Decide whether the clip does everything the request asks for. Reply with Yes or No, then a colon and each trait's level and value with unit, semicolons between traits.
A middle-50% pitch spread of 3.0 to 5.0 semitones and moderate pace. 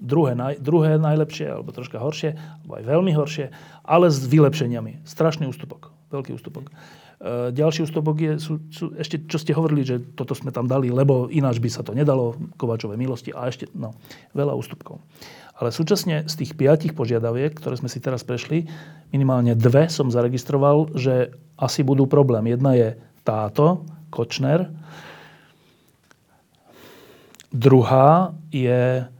Yes: average, 3.8 semitones; average, 140 wpm